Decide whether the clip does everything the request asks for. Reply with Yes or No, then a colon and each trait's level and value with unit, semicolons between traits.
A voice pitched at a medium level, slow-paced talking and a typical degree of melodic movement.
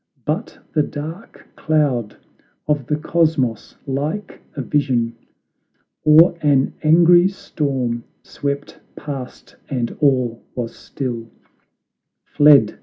Yes: medium, 145 Hz; slow, 100 wpm; average, 3.7 semitones